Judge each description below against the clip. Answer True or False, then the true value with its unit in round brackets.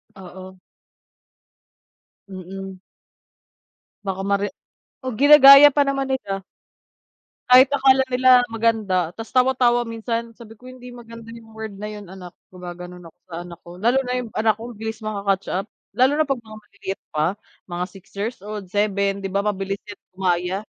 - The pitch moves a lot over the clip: False (4.0 semitones)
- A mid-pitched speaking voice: False (210 Hz)